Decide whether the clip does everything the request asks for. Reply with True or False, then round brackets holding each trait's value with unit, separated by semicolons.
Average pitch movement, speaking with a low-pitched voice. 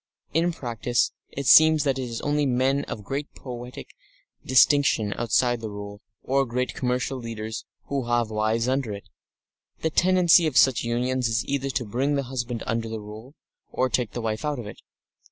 True (3.2 semitones; 125 Hz)